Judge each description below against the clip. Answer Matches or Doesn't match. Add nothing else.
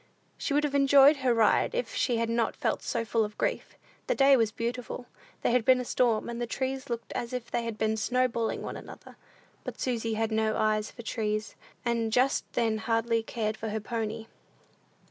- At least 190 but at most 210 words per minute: Matches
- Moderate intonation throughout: Doesn't match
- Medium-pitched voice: Doesn't match